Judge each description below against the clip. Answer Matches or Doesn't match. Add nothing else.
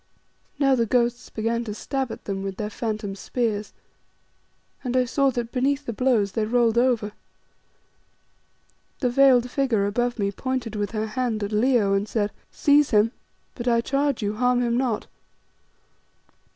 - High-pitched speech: Matches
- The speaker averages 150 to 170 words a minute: Matches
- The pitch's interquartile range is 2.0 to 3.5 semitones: Matches